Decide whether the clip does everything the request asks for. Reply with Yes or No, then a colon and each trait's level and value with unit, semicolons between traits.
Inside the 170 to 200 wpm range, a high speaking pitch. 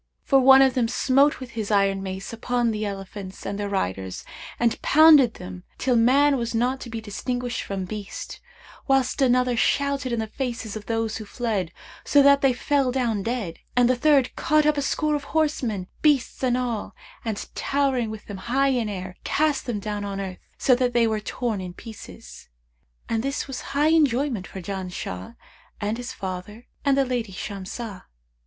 Yes: average, 185 wpm; high, 235 Hz